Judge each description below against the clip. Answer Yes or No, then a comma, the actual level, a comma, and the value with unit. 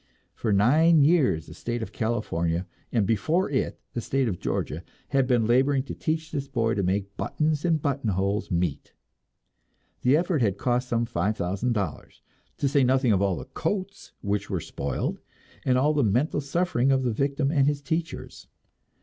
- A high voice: No, low, 125 Hz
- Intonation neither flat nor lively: No, wide, 5.8 semitones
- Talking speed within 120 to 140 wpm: No, average, 175 wpm